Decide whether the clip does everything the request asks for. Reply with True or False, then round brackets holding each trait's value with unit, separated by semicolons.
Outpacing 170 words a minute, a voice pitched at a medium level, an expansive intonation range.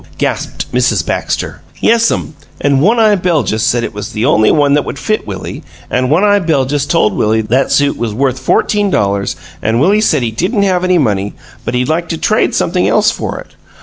True (205 wpm; 145 Hz; 7.8 semitones)